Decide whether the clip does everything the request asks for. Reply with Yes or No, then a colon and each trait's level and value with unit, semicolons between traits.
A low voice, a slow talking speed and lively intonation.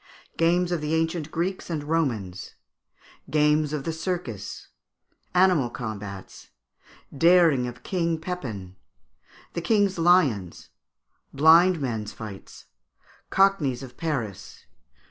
No: medium, 155 Hz; slow, 105 wpm; wide, 6.2 semitones